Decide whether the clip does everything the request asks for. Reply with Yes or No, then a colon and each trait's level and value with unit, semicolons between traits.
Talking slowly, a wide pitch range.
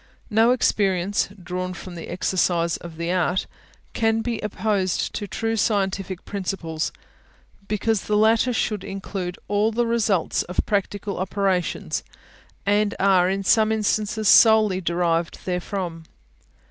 No: slow, 125 wpm; average, 3.1 semitones